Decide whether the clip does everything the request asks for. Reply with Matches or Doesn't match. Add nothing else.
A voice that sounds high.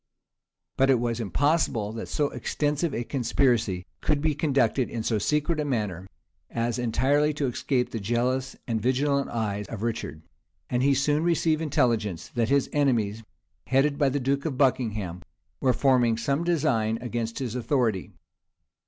Doesn't match